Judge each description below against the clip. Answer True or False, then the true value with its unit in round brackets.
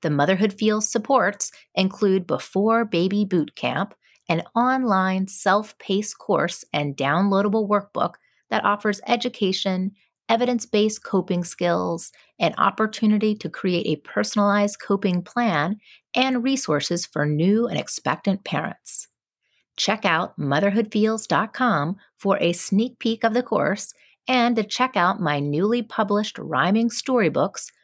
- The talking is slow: True (125 wpm)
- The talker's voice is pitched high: True (205 Hz)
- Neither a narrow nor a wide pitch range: True (4.1 semitones)